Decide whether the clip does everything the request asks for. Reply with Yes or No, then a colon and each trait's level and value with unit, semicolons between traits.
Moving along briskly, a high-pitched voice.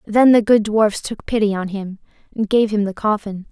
Yes: fast, 220 wpm; high, 210 Hz